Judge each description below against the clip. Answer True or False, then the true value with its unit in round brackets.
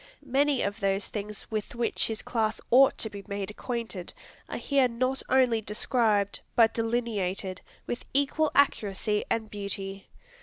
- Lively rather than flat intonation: False (3.5 semitones)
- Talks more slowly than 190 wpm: True (145 wpm)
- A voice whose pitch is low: False (220 Hz)